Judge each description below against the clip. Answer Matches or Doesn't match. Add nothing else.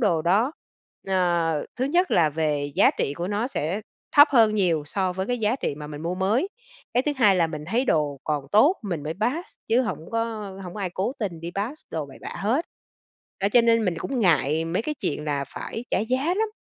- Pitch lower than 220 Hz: Matches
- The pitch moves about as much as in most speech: Doesn't match